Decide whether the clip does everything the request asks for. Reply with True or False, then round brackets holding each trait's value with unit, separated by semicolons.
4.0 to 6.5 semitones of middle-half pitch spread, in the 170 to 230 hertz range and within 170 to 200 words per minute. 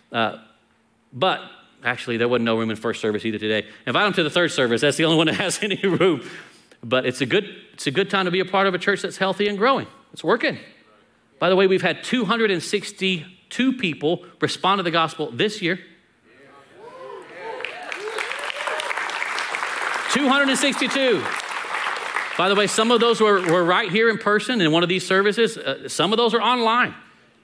True (5.6 semitones; 190 Hz; 180 wpm)